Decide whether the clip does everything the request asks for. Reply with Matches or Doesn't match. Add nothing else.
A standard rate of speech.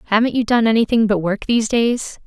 Doesn't match